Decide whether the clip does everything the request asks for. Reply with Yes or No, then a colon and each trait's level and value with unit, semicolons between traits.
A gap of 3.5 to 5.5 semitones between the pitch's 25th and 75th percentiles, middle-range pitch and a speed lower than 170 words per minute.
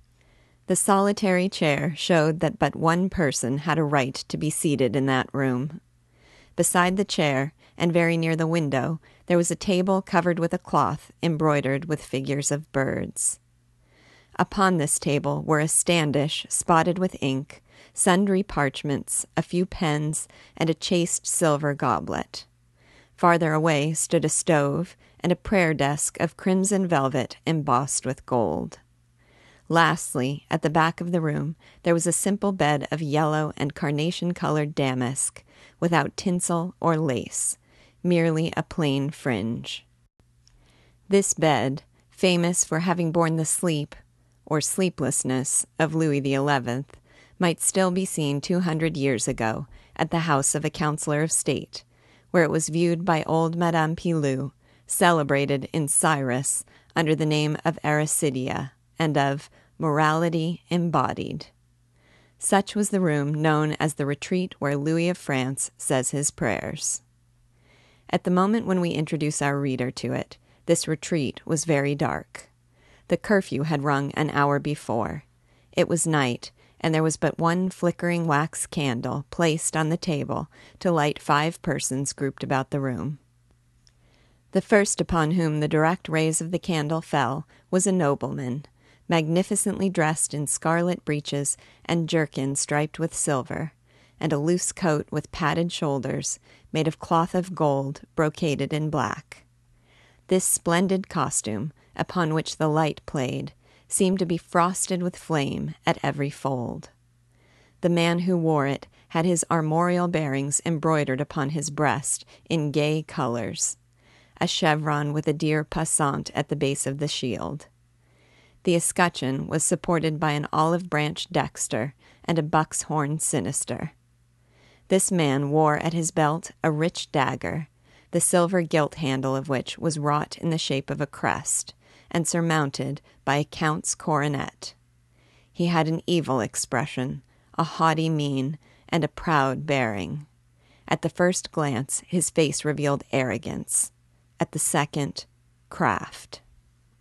Yes: average, 3.8 semitones; medium, 150 Hz; average, 145 wpm